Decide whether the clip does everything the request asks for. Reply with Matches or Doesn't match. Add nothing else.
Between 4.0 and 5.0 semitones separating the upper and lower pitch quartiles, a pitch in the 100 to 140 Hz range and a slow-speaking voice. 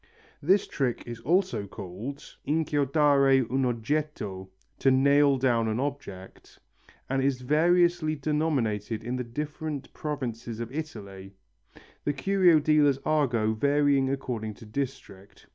Matches